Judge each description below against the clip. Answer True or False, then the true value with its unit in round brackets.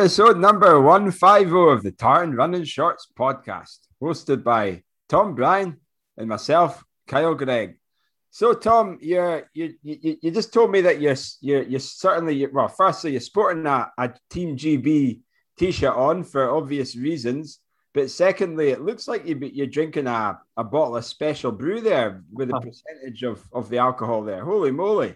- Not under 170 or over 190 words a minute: False (160 wpm)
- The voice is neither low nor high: True (150 Hz)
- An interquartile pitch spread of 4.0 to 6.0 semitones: True (5.4 semitones)